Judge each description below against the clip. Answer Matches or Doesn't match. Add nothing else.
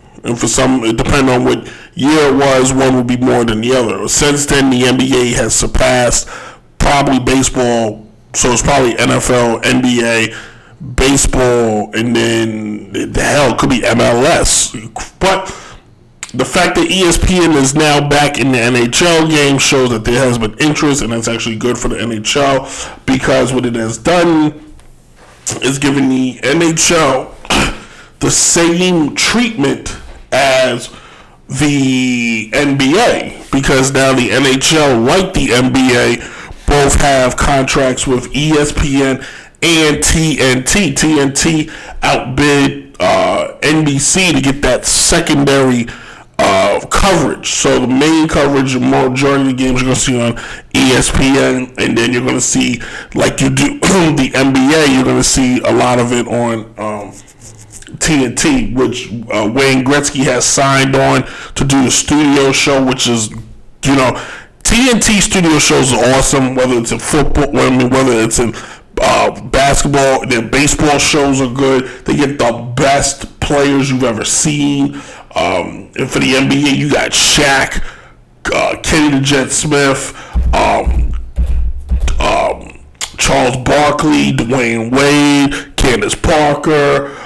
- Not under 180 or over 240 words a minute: Doesn't match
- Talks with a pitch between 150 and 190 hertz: Doesn't match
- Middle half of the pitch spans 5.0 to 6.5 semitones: Doesn't match